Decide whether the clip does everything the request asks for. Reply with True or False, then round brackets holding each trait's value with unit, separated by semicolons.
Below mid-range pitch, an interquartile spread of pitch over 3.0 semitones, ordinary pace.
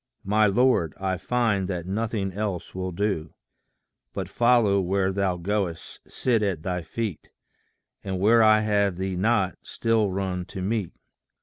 False (100 Hz; 2.7 semitones; 145 wpm)